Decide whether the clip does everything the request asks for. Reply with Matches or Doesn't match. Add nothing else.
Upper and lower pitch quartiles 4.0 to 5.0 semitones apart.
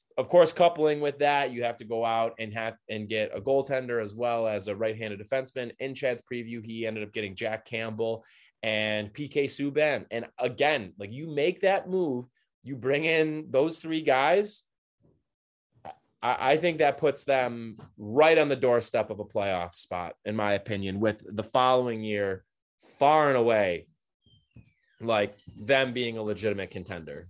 Matches